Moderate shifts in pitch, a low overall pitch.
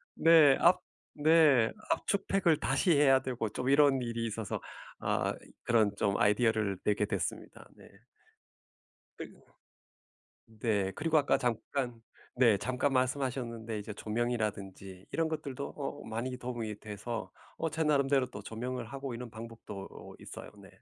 Yes: average, 4.3 semitones; low, 120 Hz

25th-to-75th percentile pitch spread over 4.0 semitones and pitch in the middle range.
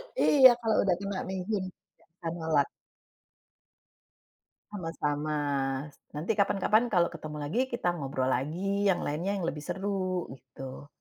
Yes: average, 4.8 semitones; medium, 175 Hz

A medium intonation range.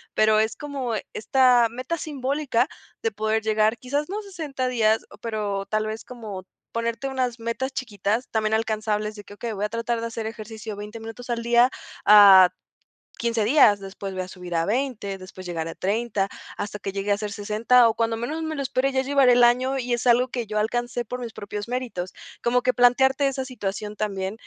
Yes: average, 3.2 semitones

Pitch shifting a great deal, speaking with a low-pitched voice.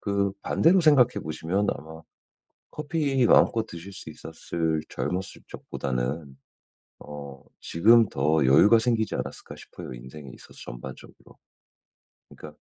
Yes: wide, 7.5 semitones; very low, 85 Hz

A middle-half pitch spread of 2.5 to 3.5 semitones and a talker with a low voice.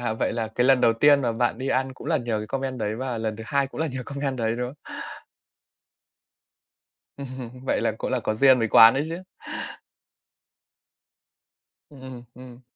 Yes: average, 2.9 semitones; low, 125 Hz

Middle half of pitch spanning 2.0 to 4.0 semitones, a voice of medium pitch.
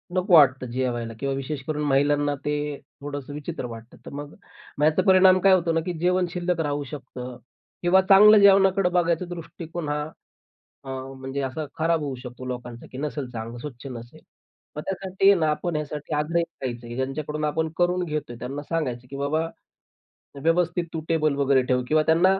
No: average, 4.4 semitones; medium, 150 Hz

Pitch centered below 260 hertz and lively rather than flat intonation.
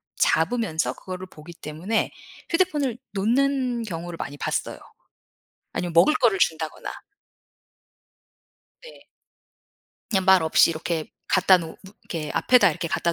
Yes: medium, 185 Hz; wide, 6.4 semitones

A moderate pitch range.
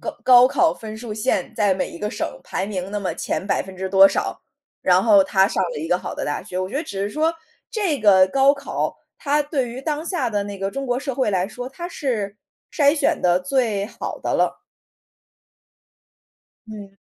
No: wide, 5.9 semitones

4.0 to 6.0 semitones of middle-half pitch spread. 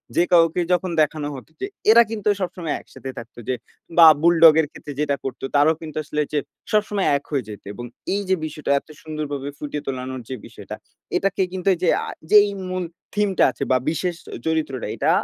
Yes: average, 4.3 semitones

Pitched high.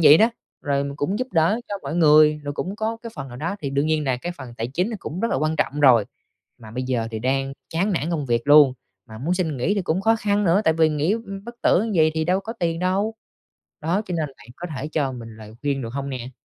No: medium, 155 Hz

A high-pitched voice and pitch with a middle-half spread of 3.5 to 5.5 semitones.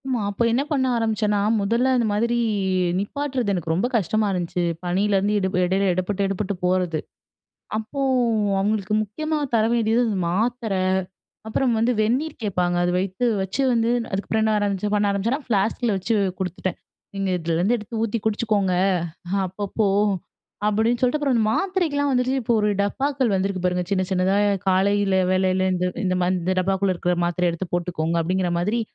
Yes: high, 205 Hz; average, 3.8 semitones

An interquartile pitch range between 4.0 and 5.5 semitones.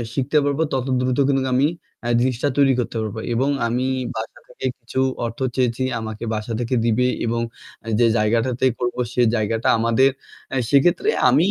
No: narrow, 2.6 semitones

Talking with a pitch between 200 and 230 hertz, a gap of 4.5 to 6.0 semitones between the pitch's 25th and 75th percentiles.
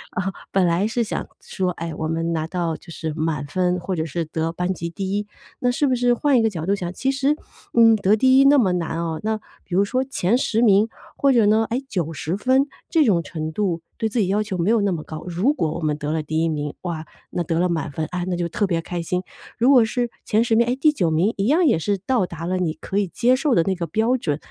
No: medium, 185 Hz; wide, 5.6 semitones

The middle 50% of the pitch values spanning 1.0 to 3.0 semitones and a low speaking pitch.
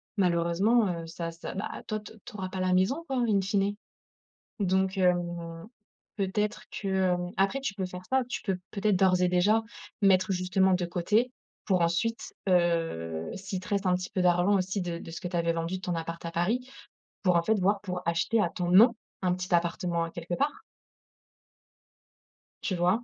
No: narrow, 2.5 semitones; medium, 185 Hz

